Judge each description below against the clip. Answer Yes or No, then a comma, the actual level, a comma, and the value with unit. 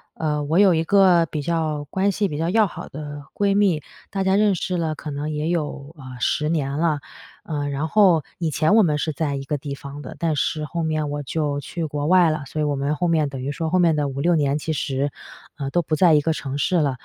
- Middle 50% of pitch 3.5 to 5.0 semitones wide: No, average, 2.8 semitones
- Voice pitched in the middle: Yes, medium, 155 Hz